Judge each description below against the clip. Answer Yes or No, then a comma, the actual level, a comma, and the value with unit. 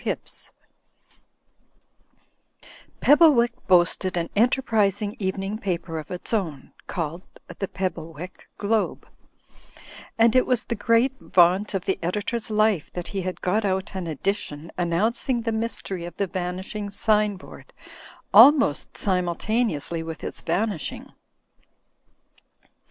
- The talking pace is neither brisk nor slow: No, slow, 115 wpm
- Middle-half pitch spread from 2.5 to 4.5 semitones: Yes, average, 4.0 semitones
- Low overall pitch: No, high, 195 Hz